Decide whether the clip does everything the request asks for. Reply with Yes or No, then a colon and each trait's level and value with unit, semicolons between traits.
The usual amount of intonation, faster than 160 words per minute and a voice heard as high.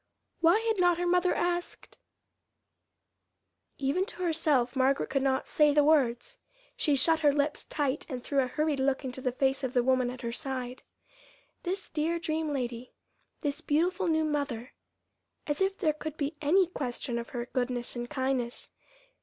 Yes: average, 4.0 semitones; average, 170 wpm; very high, 285 Hz